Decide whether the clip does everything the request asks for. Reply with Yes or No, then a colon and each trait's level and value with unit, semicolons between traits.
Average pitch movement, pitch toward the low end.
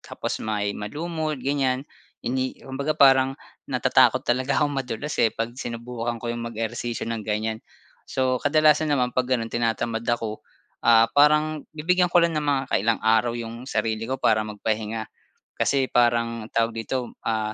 Yes: average, 3.3 semitones; low, 120 Hz